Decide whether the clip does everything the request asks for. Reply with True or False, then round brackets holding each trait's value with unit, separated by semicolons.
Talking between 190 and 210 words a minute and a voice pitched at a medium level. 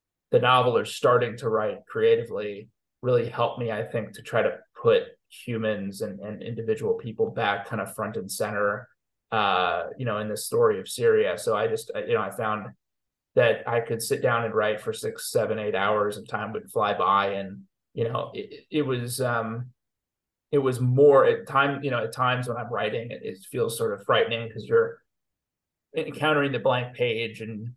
True (195 wpm; 145 Hz)